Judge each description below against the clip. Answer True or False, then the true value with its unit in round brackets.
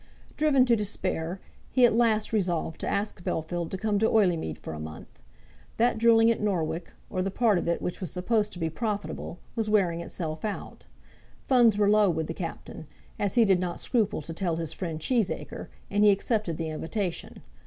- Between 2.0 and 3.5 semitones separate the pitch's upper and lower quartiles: False (4.7 semitones)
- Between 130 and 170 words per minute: False (195 wpm)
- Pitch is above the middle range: True (195 Hz)